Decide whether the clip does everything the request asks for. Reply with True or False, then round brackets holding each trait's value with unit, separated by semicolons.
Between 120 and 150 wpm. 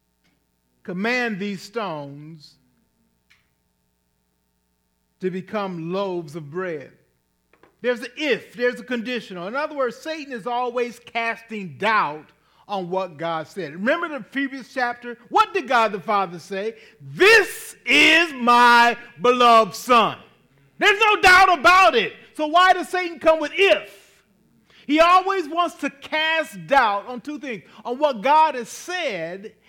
True (135 wpm)